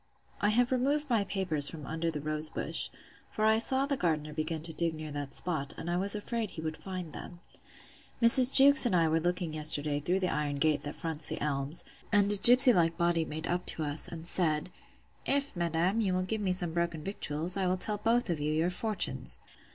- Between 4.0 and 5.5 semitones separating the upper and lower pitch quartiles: Yes, average, 4.9 semitones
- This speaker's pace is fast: Yes, fast, 215 wpm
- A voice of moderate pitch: Yes, medium, 175 Hz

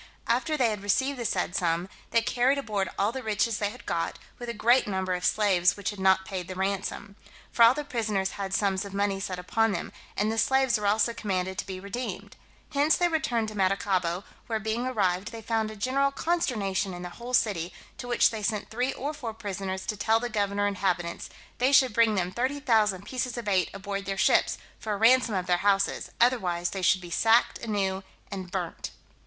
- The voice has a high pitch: Yes, high, 210 Hz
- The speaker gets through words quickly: Yes, fast, 215 wpm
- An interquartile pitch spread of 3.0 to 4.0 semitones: Yes, average, 3.7 semitones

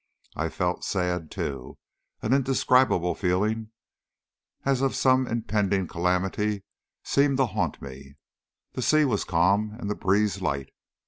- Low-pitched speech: Yes, low, 105 Hz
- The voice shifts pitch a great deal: Yes, wide, 5.7 semitones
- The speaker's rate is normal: No, slow, 130 wpm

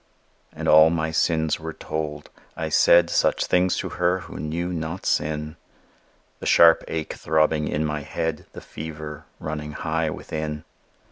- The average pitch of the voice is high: No, very low, 80 Hz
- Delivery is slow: No, average, 150 wpm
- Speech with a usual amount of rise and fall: No, narrow, 1.2 semitones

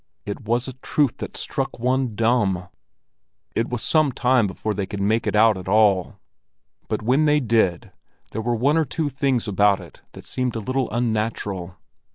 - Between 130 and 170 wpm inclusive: No, average, 185 wpm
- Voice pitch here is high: No, low, 115 Hz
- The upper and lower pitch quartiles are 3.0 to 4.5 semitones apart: Yes, average, 3.9 semitones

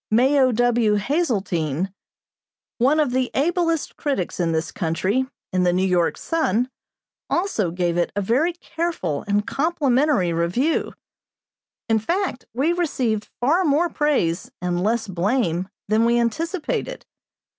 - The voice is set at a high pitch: Yes, high, 235 Hz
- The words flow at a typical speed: No, slow, 130 wpm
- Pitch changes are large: Yes, wide, 8.3 semitones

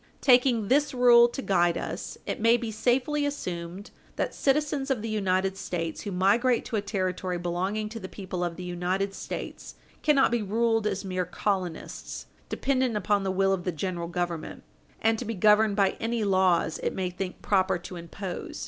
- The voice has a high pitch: Yes, high, 200 Hz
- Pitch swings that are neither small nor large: Yes, average, 4.2 semitones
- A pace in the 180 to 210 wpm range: Yes, average, 185 wpm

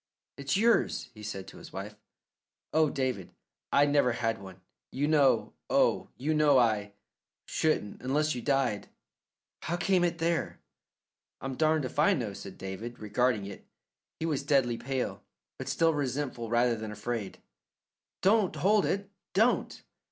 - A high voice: No, low, 135 Hz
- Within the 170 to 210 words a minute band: No, average, 150 wpm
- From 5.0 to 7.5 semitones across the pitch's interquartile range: Yes, wide, 5.6 semitones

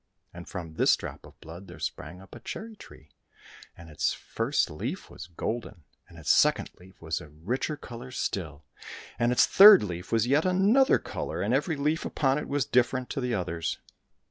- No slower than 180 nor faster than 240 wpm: Yes, average, 190 wpm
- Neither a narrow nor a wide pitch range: No, wide, 8.6 semitones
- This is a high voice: No, low, 115 Hz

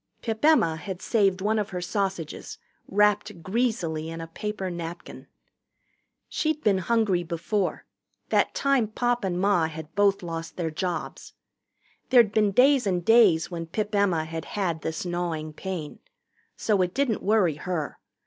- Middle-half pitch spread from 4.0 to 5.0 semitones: Yes, average, 4.4 semitones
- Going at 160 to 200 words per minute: No, average, 150 wpm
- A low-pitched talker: No, high, 190 Hz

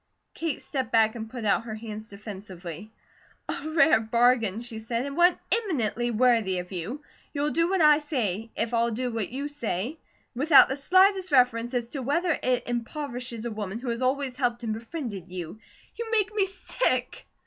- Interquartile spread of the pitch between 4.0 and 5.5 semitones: Yes, average, 4.8 semitones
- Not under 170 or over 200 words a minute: Yes, average, 180 wpm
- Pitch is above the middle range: Yes, high, 240 Hz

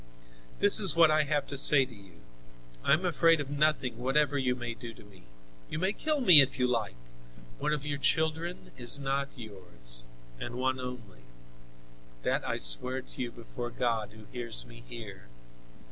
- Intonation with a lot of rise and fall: No, average, 4.5 semitones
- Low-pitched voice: Yes, low, 130 Hz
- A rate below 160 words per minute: No, average, 180 wpm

